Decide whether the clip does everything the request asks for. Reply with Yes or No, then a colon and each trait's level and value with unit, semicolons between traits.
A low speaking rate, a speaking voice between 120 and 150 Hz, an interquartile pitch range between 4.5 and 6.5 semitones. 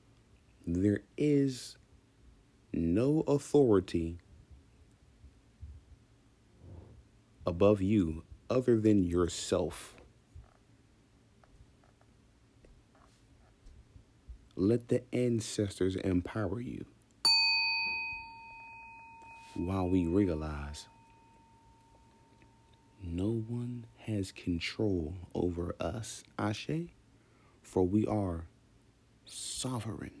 No: slow, 55 wpm; low, 110 Hz; average, 5.3 semitones